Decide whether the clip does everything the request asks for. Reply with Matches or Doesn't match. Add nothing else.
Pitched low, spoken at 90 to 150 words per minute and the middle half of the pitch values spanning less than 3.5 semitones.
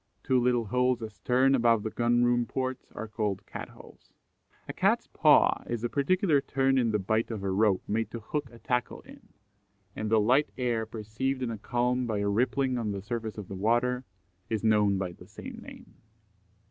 Doesn't match